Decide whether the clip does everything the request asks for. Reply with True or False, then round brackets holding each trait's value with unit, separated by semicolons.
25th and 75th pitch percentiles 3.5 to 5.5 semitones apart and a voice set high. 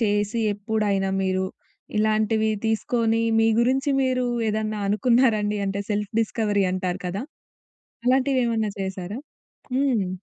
False (2.6 semitones; 215 Hz)